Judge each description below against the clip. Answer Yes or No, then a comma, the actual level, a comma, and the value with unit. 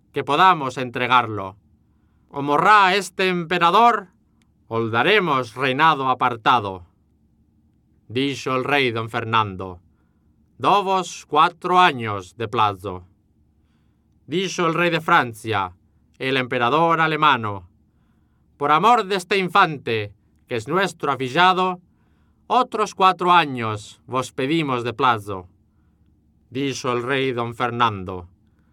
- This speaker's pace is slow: Yes, slow, 105 wpm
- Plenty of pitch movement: Yes, wide, 8.6 semitones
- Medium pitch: No, low, 125 Hz